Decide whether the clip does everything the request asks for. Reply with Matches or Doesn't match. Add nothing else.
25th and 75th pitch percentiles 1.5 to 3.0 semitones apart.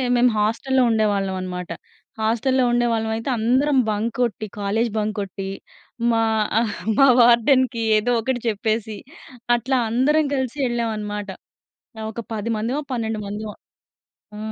Matches